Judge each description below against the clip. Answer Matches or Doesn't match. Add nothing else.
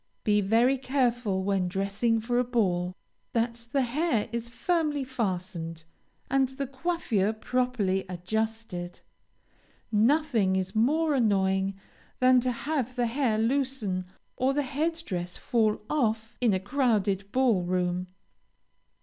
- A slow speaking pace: Matches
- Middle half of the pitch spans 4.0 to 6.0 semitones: Matches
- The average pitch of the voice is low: Doesn't match